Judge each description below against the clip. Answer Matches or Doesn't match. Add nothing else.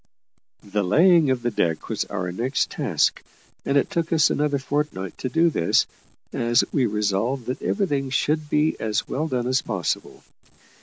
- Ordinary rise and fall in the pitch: Doesn't match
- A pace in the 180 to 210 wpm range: Doesn't match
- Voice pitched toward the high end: Doesn't match